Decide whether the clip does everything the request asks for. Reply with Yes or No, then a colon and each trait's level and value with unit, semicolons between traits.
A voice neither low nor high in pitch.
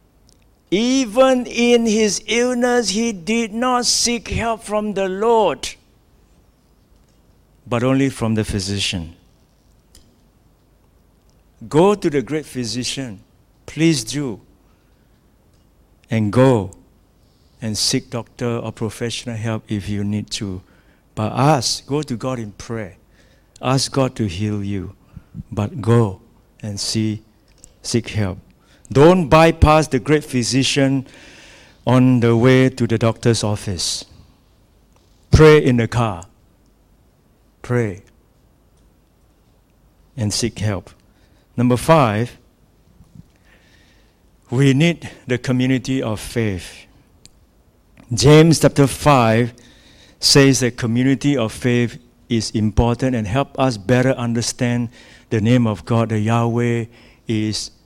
No: low, 120 Hz